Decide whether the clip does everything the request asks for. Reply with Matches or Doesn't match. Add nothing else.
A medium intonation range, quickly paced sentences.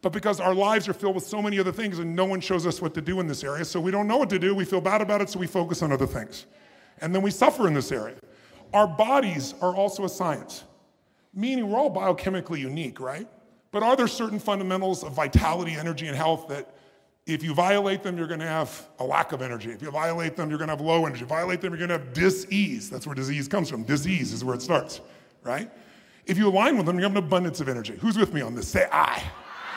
Matches